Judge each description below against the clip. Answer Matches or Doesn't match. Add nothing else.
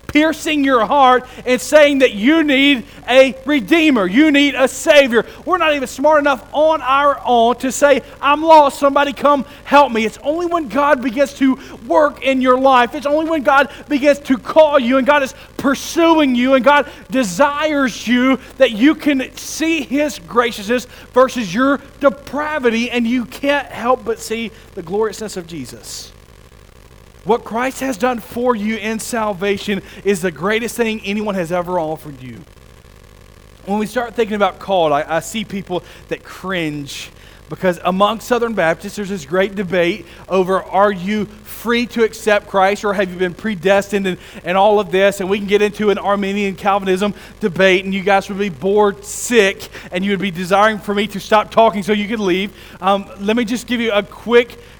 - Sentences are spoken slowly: Doesn't match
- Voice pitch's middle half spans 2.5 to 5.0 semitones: Doesn't match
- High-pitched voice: Matches